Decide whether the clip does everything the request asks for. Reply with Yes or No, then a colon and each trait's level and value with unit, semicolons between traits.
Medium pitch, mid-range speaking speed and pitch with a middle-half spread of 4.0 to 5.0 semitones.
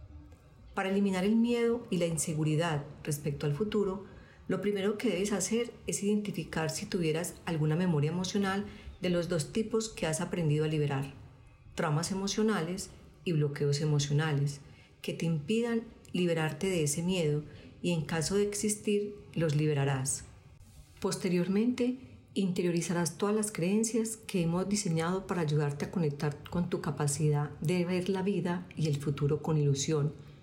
Yes: medium, 175 Hz; average, 145 wpm; average, 4.7 semitones